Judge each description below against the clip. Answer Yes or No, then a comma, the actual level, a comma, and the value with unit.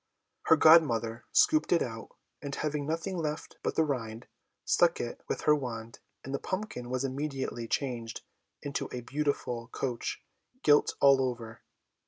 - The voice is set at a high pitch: No, low, 135 Hz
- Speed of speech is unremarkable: Yes, average, 150 wpm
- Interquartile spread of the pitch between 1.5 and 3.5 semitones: No, average, 4.2 semitones